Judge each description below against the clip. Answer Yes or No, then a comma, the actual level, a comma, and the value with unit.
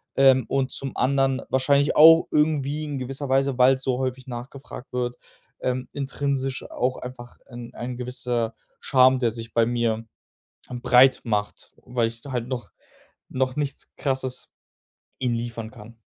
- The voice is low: Yes, low, 130 Hz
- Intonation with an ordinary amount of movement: No, narrow, 1.9 semitones